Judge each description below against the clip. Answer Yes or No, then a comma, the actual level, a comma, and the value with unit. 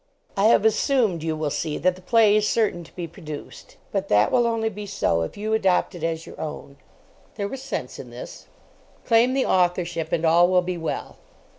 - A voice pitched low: No, medium, 185 Hz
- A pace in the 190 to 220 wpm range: Yes, fast, 205 wpm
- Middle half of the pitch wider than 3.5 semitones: Yes, average, 5.1 semitones